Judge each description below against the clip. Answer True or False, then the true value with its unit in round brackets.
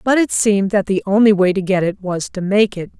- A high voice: True (200 Hz)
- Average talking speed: False (280 wpm)